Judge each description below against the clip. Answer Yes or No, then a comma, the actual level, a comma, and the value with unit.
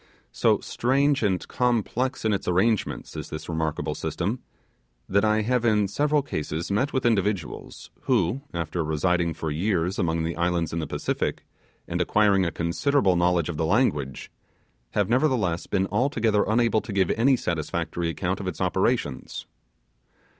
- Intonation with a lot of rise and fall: Yes, wide, 5.7 semitones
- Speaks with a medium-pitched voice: No, very low, 95 Hz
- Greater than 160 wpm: No, average, 155 wpm